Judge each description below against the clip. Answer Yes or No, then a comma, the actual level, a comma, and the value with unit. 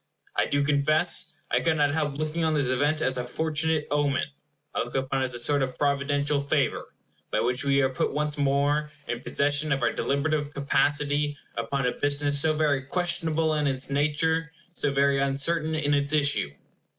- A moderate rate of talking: Yes, average, 185 wpm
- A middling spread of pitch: No, narrow, 1.7 semitones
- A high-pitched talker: No, medium, 145 Hz